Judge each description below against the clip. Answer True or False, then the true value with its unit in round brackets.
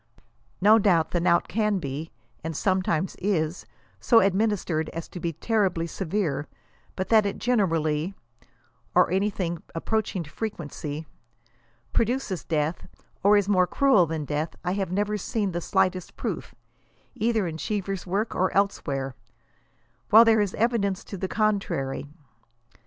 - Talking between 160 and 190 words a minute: False (140 wpm)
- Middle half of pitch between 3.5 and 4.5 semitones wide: True (4.2 semitones)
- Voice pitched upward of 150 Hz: True (185 Hz)